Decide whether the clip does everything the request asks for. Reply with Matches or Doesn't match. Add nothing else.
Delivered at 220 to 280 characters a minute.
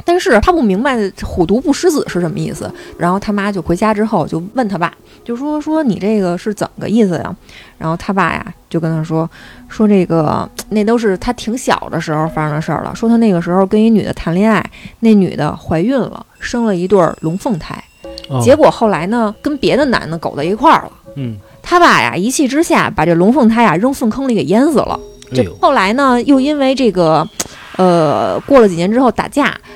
Doesn't match